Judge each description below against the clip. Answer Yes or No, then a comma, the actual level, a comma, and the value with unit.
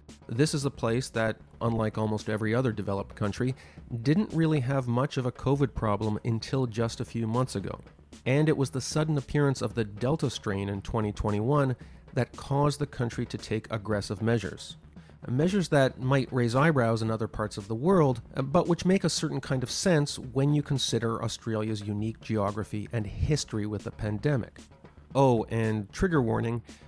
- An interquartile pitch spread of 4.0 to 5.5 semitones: Yes, average, 4.3 semitones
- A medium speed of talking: Yes, average, 175 wpm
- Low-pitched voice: Yes, low, 120 Hz